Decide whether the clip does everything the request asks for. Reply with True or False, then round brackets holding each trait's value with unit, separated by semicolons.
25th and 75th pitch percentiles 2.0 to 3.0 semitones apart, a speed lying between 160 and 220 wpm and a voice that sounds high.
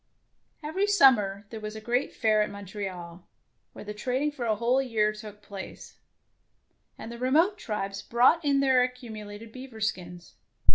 False (3.9 semitones; 170 wpm; 220 Hz)